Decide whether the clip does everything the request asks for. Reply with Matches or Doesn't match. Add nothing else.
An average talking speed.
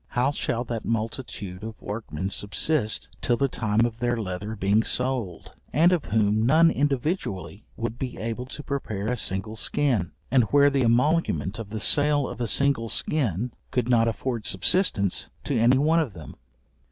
Matches